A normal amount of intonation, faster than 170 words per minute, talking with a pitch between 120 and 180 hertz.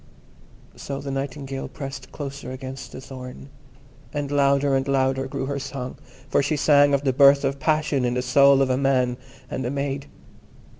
No: narrow, 1.1 semitones; average, 180 wpm; low, 135 Hz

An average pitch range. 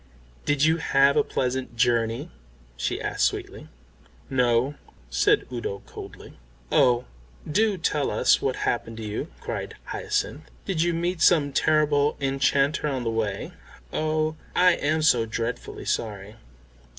Yes: average, 5.0 semitones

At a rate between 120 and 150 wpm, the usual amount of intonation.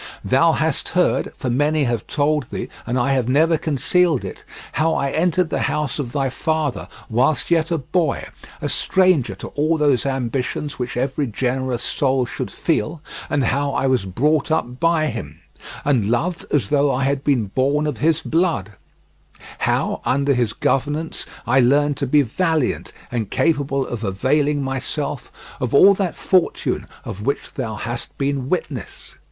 No: average, 160 wpm; average, 3.6 semitones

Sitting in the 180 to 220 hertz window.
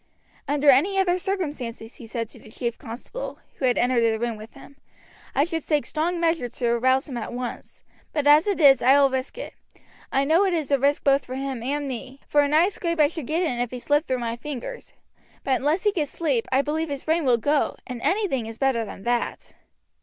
No: very high, 275 Hz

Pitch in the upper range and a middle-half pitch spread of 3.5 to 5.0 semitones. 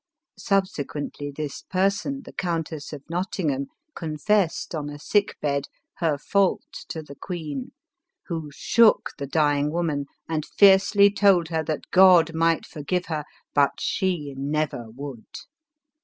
No: medium, 160 Hz; average, 4.2 semitones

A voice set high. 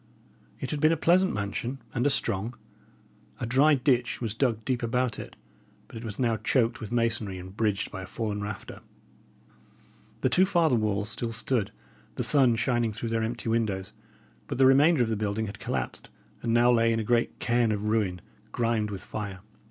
No: low, 115 Hz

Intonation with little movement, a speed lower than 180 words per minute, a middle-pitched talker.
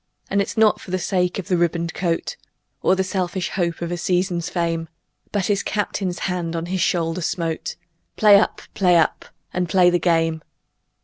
No: narrow, 2.0 semitones; average, 185 wpm; medium, 180 Hz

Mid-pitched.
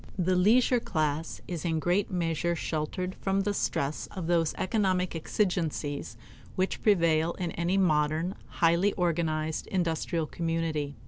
Yes: medium, 170 Hz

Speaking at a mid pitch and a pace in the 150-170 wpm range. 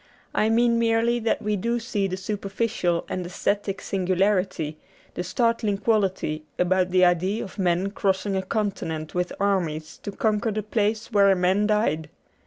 No: high, 195 Hz; average, 160 wpm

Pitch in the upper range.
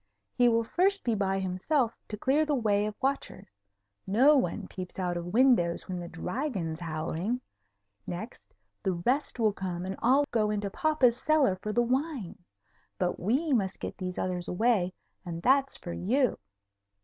Yes: high, 210 Hz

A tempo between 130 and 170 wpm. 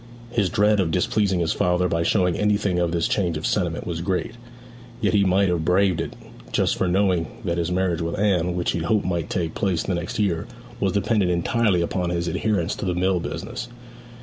No: fast, 205 wpm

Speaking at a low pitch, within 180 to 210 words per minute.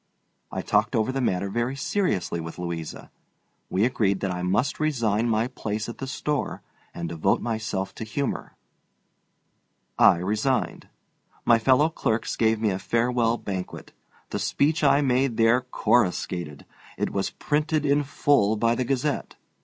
No: low, 115 Hz; average, 150 wpm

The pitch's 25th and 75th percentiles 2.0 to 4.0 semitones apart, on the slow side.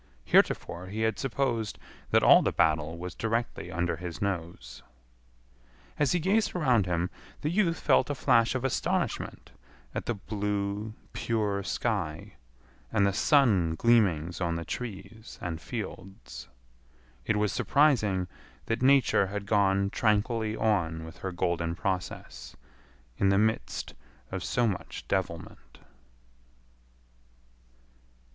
No: average, 4.5 semitones; slow, 125 wpm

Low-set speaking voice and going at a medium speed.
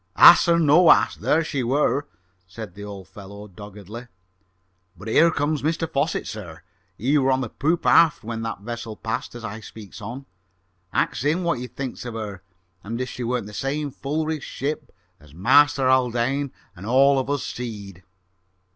Yes: low, 125 Hz; average, 180 wpm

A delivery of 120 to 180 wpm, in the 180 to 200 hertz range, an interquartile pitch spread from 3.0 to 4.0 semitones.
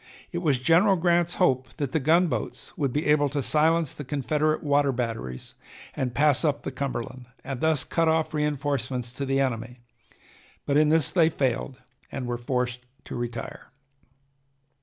No: average, 160 wpm; medium, 140 Hz; average, 3.7 semitones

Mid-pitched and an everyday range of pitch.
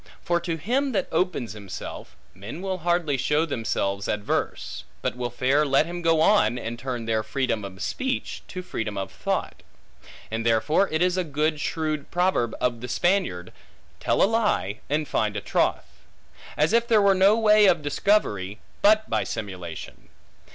No: medium, 150 Hz; wide, 8.5 semitones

